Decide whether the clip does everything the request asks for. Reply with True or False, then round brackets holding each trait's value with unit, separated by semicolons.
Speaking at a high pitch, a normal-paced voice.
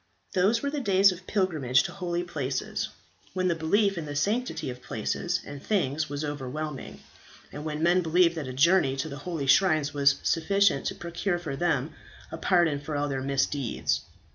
False (160 Hz; 185 wpm)